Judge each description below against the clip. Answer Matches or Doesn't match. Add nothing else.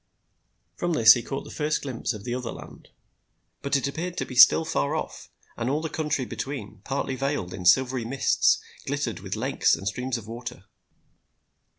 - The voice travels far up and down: Doesn't match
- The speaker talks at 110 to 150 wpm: Doesn't match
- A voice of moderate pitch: Doesn't match